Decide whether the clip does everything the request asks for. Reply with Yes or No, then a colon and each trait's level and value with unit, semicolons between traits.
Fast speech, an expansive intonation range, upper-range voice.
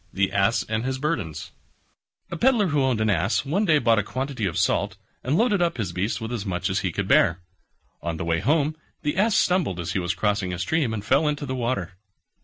No: fast, 230 wpm; wide, 7.8 semitones; low, 115 Hz